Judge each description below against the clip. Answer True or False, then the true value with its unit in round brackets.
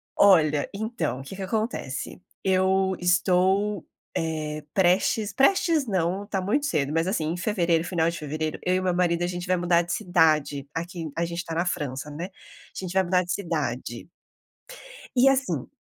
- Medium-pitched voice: True (175 Hz)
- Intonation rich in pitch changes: False (3.0 semitones)